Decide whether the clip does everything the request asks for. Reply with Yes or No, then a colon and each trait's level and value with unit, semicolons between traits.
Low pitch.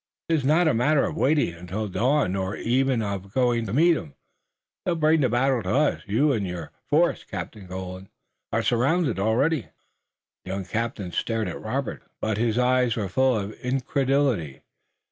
Yes: low, 120 Hz